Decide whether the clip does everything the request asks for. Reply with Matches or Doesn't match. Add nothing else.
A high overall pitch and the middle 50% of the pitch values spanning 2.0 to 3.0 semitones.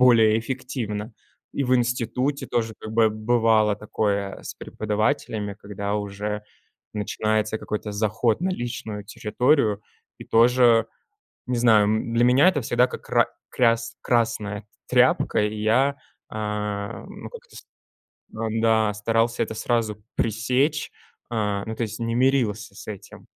Doesn't match